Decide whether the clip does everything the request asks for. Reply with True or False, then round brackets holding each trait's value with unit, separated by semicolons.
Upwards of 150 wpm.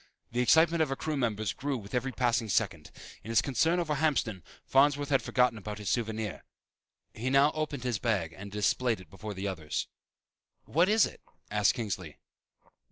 True (175 wpm)